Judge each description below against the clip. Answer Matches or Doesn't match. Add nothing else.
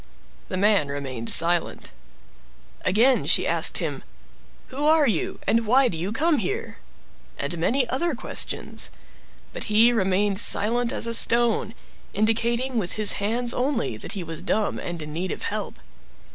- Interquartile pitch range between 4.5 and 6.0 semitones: Matches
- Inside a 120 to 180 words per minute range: Matches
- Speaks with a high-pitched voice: Matches